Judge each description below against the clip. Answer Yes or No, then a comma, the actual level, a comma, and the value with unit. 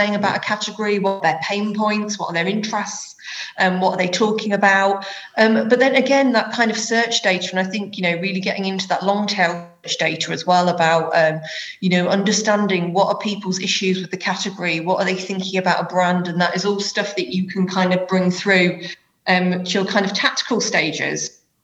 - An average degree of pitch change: No, narrow, 2.3 semitones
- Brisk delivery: Yes, fast, 220 wpm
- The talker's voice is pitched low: No, high, 195 Hz